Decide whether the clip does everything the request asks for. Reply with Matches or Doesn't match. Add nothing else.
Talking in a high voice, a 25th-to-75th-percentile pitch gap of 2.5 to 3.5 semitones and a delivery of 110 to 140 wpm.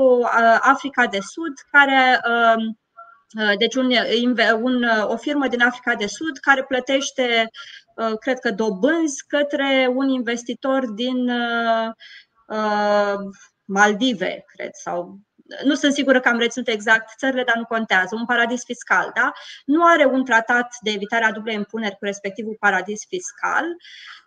Matches